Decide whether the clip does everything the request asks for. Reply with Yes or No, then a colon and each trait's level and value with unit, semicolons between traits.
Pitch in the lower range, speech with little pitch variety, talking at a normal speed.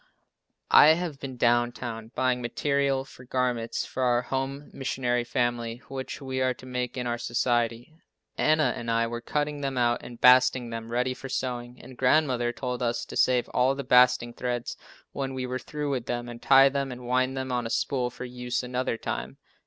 Yes: low, 125 Hz; narrow, 1.6 semitones; average, 195 wpm